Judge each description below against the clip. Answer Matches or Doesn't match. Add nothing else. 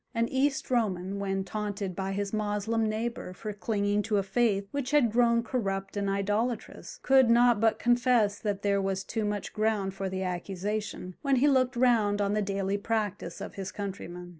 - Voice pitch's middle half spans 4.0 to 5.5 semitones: Doesn't match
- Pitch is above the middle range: Matches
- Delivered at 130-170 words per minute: Doesn't match